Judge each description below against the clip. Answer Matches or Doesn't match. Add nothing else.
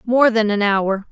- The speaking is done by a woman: Matches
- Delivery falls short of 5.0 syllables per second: Matches